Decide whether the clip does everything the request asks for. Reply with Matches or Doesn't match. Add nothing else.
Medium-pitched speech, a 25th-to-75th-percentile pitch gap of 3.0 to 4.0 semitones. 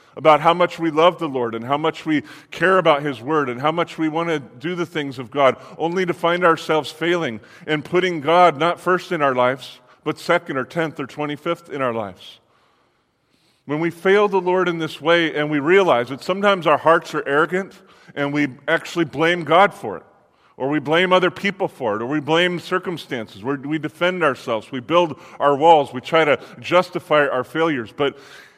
Matches